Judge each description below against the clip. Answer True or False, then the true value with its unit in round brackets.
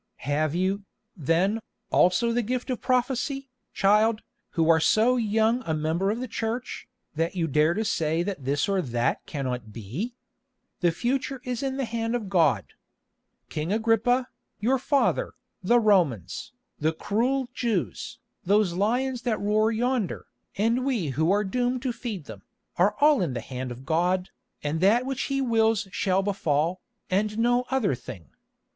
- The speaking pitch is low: False (205 Hz)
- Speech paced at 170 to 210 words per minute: False (160 wpm)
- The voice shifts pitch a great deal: True (6.7 semitones)